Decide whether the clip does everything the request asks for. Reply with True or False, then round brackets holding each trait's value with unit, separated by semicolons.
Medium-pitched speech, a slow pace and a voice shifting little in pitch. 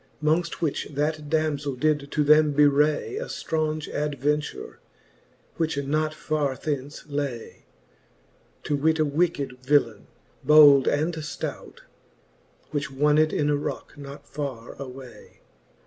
True (150 Hz; 120 wpm; 1.6 semitones)